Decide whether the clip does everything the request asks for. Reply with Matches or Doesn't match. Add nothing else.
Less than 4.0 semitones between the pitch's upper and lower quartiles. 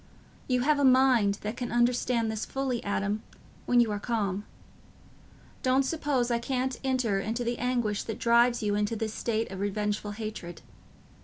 Matches